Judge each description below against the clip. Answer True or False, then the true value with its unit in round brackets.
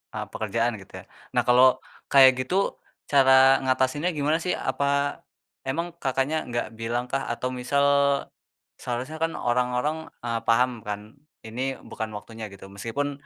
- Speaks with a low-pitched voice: True (130 Hz)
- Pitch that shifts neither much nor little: True (3.1 semitones)